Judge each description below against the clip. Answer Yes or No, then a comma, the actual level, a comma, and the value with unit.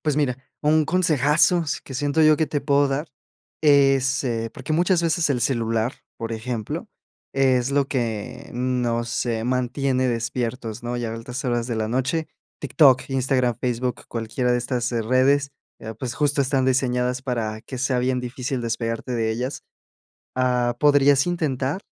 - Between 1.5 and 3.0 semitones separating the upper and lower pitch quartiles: Yes, average, 2.7 semitones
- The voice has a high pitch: No, low, 130 Hz